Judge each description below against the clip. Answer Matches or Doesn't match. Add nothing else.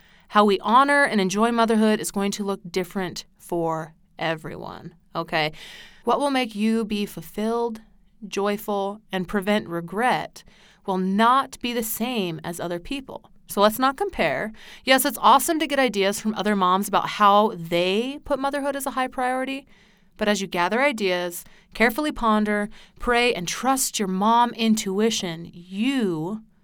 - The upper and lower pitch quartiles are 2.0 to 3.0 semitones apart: Doesn't match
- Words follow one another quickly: Doesn't match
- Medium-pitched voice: Doesn't match